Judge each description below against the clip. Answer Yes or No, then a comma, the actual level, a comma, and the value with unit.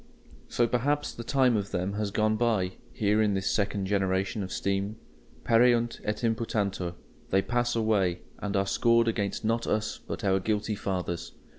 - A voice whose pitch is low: Yes, low, 105 Hz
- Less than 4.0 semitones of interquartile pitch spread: Yes, average, 2.9 semitones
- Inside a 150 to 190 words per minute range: Yes, average, 165 wpm